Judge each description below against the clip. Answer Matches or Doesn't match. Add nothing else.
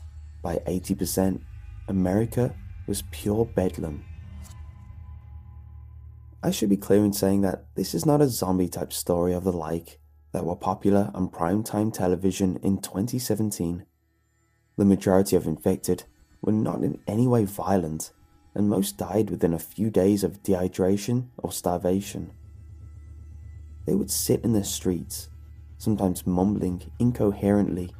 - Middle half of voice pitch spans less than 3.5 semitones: Matches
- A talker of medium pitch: Doesn't match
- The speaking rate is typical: Doesn't match